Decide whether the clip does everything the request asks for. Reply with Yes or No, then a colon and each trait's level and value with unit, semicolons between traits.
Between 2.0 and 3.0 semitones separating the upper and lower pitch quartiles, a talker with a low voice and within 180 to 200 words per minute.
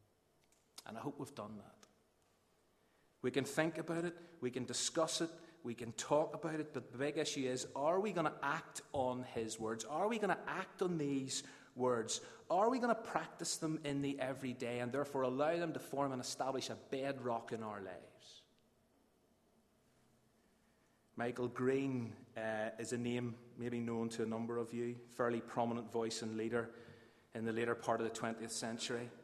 No: average, 3.4 semitones; low, 125 Hz; average, 185 wpm